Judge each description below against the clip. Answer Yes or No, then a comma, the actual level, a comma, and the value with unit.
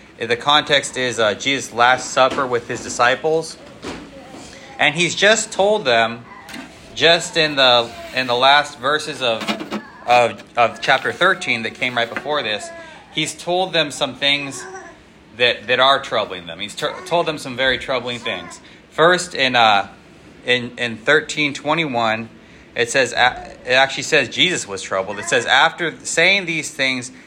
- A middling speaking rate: Yes, average, 155 wpm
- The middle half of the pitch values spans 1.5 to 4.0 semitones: No, average, 4.5 semitones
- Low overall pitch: Yes, low, 130 Hz